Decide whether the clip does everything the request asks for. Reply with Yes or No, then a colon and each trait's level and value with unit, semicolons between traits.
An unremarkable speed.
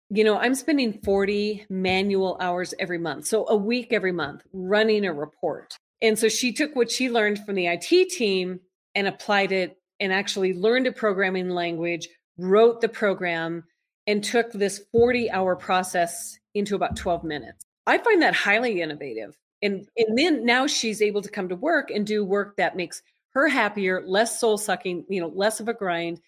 Yes: average, 185 wpm